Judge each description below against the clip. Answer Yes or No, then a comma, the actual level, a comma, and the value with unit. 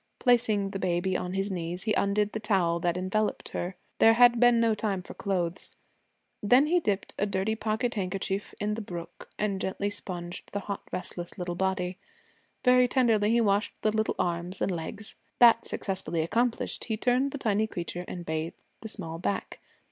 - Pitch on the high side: Yes, high, 200 Hz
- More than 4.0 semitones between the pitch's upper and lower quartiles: No, average, 3.6 semitones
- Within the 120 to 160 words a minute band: No, average, 180 wpm